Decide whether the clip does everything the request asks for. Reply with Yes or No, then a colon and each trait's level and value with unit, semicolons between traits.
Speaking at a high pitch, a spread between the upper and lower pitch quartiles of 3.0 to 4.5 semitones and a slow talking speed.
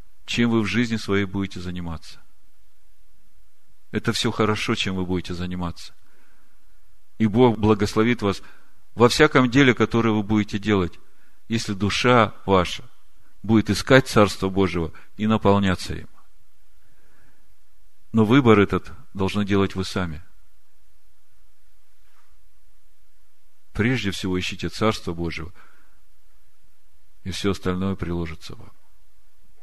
No: low, 100 Hz; average, 4.1 semitones; slow, 105 wpm